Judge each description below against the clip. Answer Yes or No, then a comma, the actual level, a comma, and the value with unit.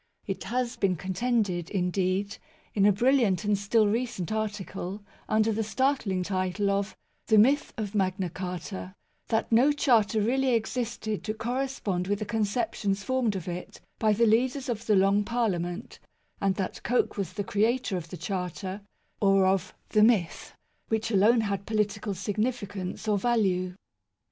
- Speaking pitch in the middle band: No, high, 205 Hz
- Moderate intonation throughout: Yes, average, 3.2 semitones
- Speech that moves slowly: No, average, 165 wpm